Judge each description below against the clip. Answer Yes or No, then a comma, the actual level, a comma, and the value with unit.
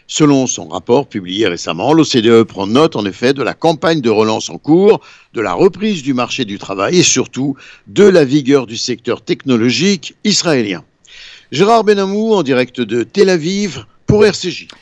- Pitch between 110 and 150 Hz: Yes, low, 135 Hz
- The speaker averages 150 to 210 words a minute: Yes, fast, 170 wpm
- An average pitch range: No, wide, 7.5 semitones